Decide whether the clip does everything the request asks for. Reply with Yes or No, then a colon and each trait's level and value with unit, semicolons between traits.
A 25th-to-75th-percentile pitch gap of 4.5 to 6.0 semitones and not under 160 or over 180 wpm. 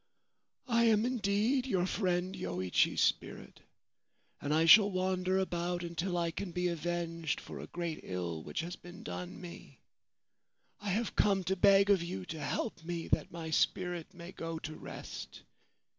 No: average, 2.8 semitones; average, 165 wpm